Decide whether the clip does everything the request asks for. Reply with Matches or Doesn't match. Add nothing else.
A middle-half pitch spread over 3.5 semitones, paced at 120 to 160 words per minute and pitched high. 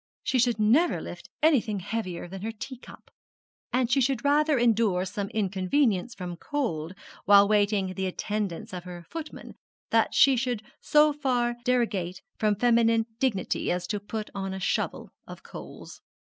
Matches